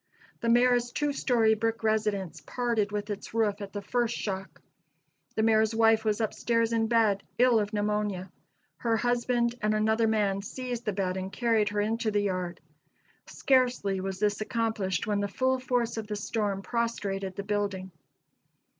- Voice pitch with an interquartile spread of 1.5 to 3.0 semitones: Yes, narrow, 2.4 semitones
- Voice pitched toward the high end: Yes, high, 215 Hz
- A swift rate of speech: No, average, 170 wpm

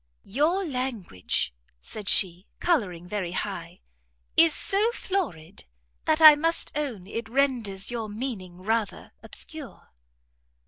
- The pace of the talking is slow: Yes, slow, 110 wpm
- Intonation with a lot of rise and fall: Yes, wide, 8.0 semitones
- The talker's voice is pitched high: Yes, high, 230 Hz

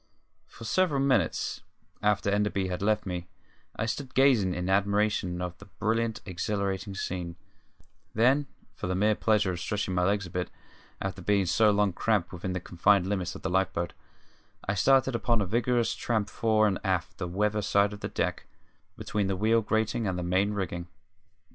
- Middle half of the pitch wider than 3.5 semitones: No, average, 3.0 semitones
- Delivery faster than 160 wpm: Yes, average, 185 wpm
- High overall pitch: No, low, 100 Hz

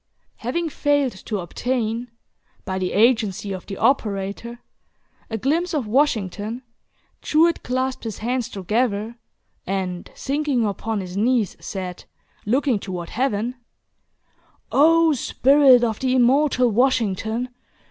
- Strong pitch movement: No, average, 4.4 semitones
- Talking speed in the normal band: No, slow, 115 wpm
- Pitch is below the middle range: No, high, 235 Hz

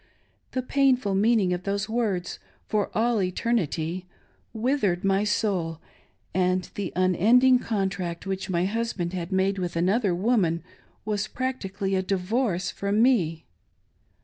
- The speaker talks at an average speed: No, slow, 125 wpm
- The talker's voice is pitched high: Yes, high, 195 Hz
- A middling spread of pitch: Yes, average, 3.8 semitones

